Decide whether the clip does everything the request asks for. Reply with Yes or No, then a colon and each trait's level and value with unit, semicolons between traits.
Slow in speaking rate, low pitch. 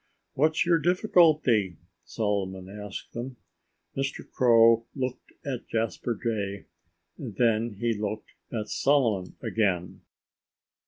Yes: slow, 105 wpm; low, 115 Hz